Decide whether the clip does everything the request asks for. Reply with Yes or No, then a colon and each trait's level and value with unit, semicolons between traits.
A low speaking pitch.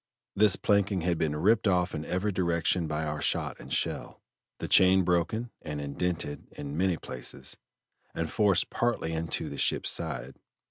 Yes: very low, 90 Hz